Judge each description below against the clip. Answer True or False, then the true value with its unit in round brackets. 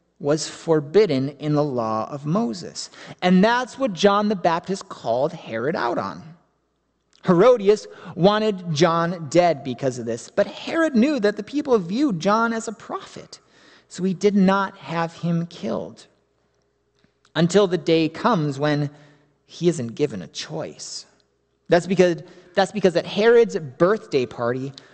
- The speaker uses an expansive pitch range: True (5.7 semitones)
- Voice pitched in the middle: True (175 Hz)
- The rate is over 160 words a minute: False (145 wpm)